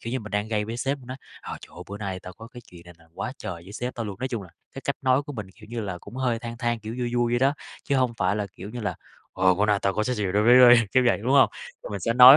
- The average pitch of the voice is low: Yes, low, 115 Hz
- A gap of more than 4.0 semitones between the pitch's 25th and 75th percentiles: No, average, 3.5 semitones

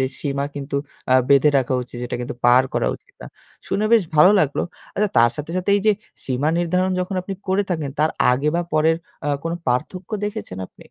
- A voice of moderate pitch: Yes, medium, 150 Hz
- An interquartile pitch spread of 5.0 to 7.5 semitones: Yes, wide, 5.5 semitones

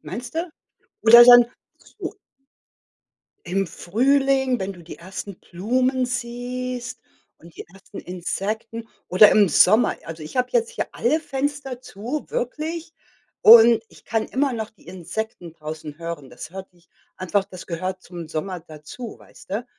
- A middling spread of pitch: No, wide, 5.8 semitones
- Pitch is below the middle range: No, high, 220 Hz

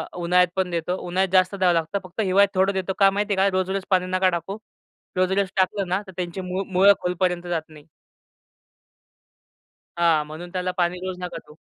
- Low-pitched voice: No, medium, 185 Hz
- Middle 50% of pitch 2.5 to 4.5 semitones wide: No, narrow, 1.5 semitones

